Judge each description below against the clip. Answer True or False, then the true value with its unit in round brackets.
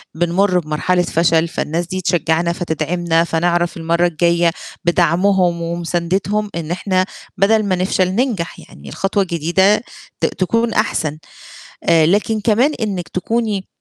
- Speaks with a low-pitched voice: False (175 Hz)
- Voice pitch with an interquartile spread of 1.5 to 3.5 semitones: True (2.7 semitones)